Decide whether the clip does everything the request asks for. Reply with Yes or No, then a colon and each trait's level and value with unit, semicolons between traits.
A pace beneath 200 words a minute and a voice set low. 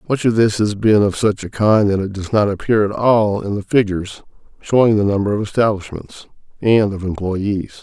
No: fast, 205 wpm; low, 105 Hz